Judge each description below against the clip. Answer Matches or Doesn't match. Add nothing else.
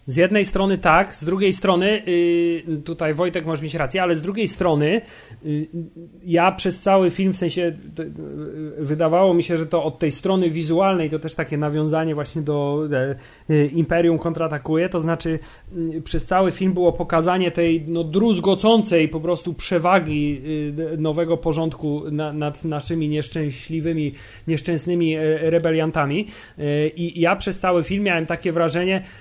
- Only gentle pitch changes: Matches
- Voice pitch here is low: Doesn't match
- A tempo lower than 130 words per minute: Doesn't match